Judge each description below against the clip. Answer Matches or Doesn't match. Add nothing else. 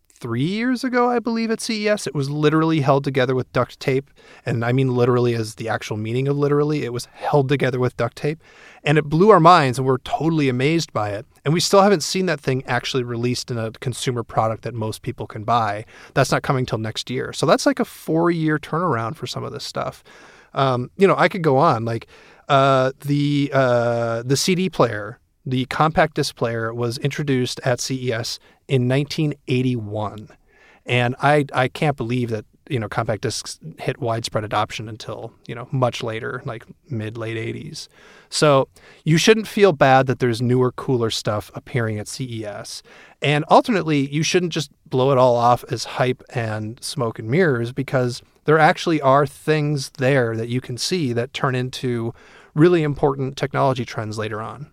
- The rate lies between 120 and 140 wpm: Doesn't match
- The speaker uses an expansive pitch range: Doesn't match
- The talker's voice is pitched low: Matches